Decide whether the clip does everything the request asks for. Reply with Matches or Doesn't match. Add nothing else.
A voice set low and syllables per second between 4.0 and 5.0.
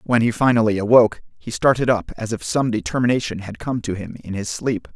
Doesn't match